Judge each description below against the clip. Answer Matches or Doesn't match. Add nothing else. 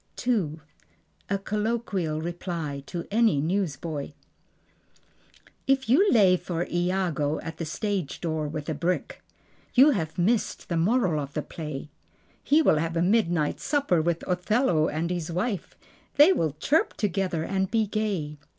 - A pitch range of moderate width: Matches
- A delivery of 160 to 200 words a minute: Doesn't match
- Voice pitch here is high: Doesn't match